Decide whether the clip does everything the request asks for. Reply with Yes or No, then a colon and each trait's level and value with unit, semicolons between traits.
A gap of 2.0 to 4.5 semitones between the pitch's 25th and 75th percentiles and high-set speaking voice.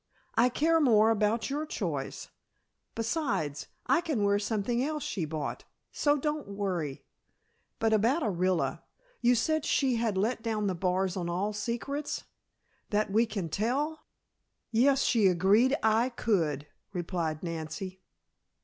No: average, 5.1 semitones; high, 215 Hz